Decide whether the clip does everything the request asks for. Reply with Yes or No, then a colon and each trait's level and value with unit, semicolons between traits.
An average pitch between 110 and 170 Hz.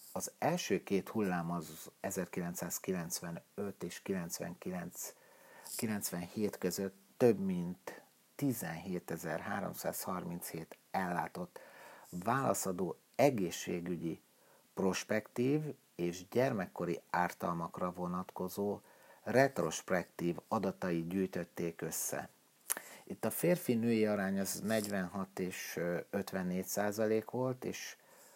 No: very low, 95 Hz